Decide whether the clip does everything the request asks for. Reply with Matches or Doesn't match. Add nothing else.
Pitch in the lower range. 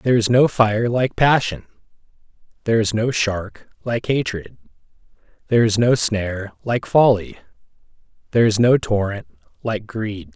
Matches